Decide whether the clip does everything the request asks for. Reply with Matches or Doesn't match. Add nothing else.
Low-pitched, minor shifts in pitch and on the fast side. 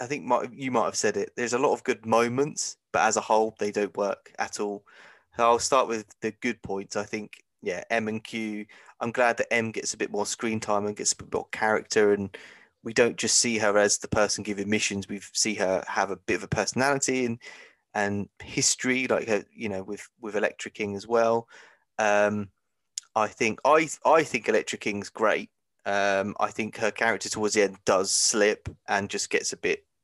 Matches